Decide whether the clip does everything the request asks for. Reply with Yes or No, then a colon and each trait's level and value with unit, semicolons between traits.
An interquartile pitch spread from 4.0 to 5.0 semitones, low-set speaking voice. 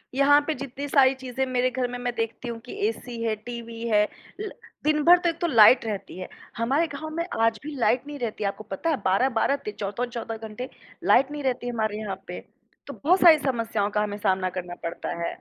No: average, 4.5 semitones; high, 240 Hz